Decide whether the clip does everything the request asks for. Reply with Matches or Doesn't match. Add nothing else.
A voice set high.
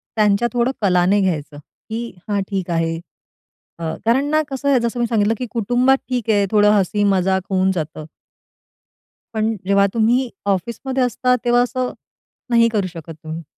Matches